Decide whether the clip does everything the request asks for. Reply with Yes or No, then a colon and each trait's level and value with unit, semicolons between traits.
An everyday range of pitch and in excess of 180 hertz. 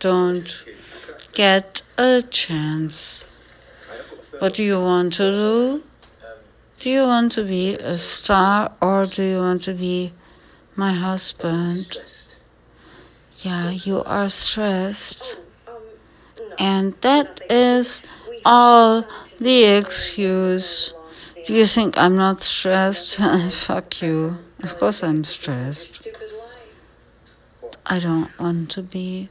Yes: average, 4.3 semitones; high, 190 Hz